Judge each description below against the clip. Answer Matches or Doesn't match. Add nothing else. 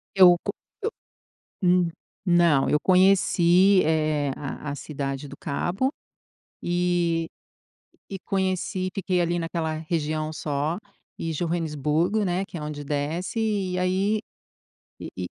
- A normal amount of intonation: Matches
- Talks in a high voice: Doesn't match